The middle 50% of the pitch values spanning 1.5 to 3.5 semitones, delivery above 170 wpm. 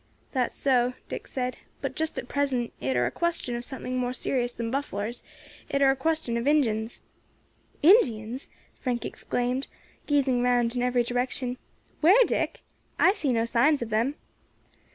No: average, 2.8 semitones; average, 160 wpm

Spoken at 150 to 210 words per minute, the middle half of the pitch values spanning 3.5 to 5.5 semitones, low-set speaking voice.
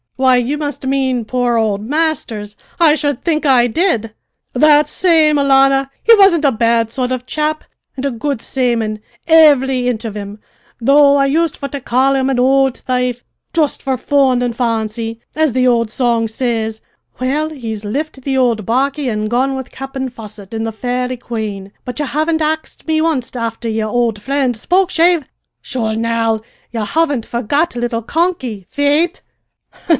No: average, 170 wpm; average, 4.0 semitones; very high, 255 Hz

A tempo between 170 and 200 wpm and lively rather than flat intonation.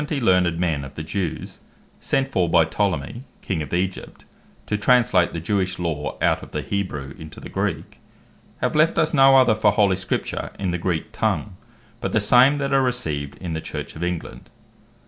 Yes: average, 185 wpm; wide, 6.4 semitones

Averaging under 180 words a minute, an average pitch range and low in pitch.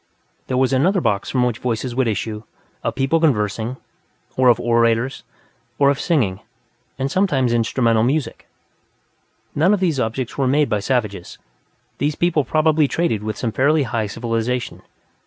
Yes: average, 155 wpm; average, 4.2 semitones; low, 125 Hz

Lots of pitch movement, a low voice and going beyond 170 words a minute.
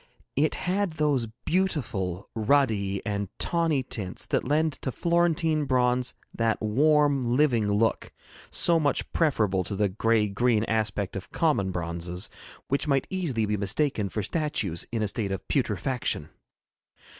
No: wide, 6.7 semitones; low, 120 Hz; average, 140 wpm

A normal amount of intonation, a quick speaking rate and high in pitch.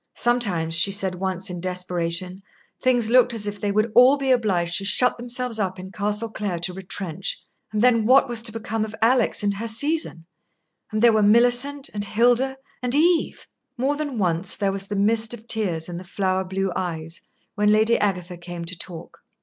No: average, 4.5 semitones; average, 195 wpm; high, 210 Hz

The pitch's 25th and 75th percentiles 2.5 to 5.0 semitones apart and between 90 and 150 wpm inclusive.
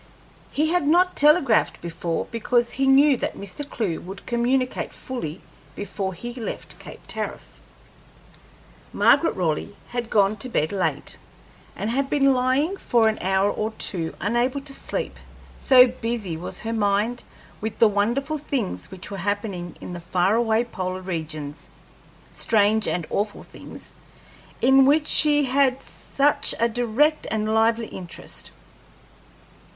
No: wide, 5.4 semitones; average, 140 wpm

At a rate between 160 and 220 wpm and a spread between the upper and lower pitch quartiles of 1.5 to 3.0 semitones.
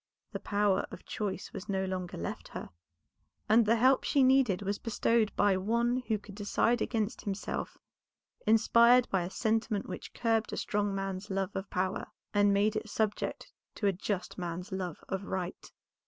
Yes: average, 170 wpm; average, 2.7 semitones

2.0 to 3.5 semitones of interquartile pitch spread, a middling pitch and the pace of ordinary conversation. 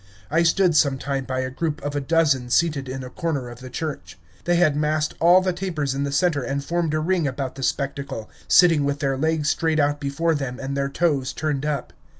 No: average, 3.1 semitones; medium, 145 Hz; fast, 225 wpm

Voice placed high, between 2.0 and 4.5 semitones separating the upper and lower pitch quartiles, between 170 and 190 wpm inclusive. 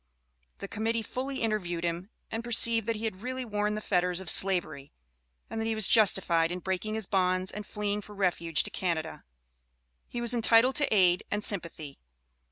Yes: high, 205 Hz; average, 3.9 semitones; average, 180 wpm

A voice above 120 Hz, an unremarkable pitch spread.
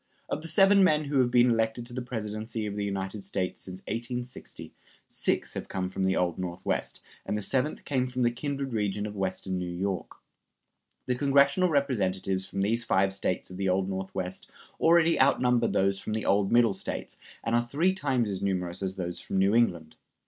No: low, 105 Hz; average, 4.8 semitones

